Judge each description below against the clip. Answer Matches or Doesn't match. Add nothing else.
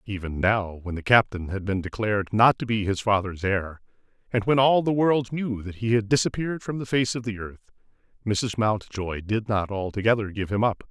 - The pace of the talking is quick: Matches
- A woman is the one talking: Doesn't match